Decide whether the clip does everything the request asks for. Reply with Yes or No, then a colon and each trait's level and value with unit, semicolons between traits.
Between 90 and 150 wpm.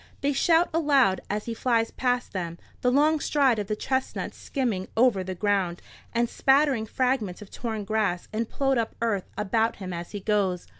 No: average, 185 wpm